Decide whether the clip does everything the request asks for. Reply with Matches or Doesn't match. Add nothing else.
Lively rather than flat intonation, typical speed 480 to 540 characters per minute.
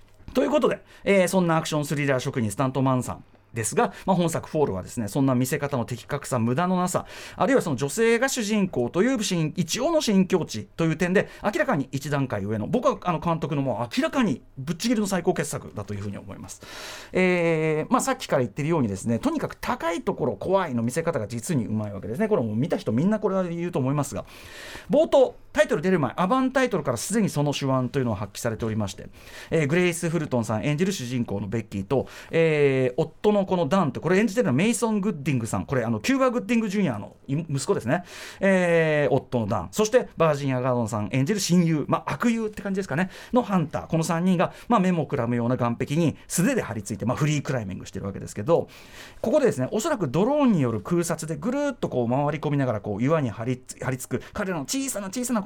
Matches